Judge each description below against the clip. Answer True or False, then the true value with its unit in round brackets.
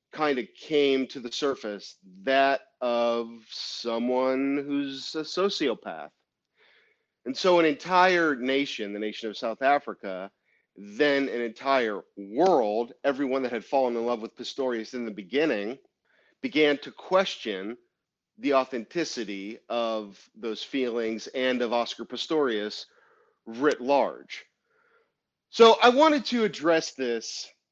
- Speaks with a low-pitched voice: True (130 Hz)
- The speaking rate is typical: False (125 wpm)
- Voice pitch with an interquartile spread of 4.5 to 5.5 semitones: True (4.9 semitones)